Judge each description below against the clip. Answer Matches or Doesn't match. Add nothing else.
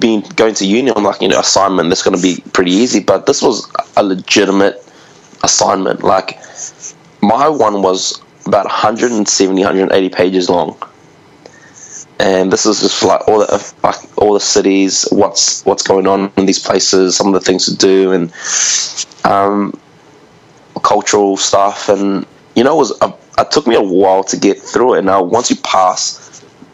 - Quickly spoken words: Doesn't match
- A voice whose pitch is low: Matches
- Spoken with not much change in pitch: Matches